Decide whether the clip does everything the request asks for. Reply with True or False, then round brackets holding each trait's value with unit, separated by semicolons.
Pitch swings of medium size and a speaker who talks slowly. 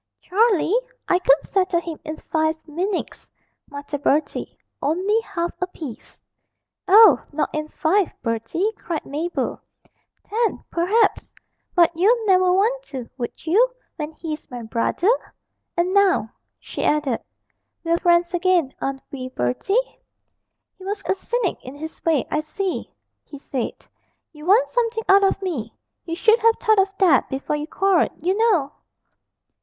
False (4.9 semitones; 145 wpm)